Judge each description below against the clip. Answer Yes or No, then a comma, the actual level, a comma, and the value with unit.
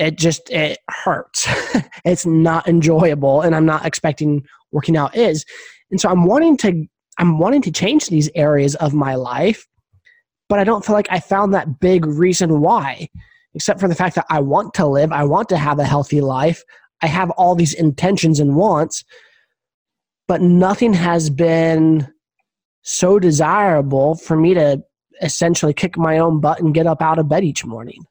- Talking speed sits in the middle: Yes, average, 180 wpm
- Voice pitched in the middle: Yes, medium, 165 Hz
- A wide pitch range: No, average, 3.2 semitones